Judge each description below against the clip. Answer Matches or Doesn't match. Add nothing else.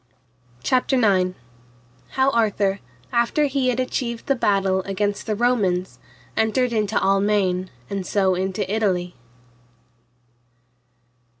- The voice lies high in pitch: Matches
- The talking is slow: Matches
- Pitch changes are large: Doesn't match